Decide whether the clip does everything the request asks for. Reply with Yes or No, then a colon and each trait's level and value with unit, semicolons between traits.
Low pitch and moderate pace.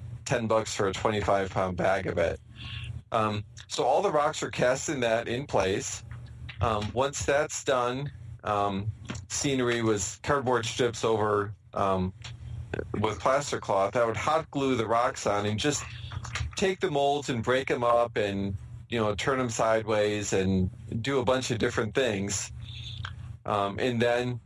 Yes: low, 115 Hz; average, 160 wpm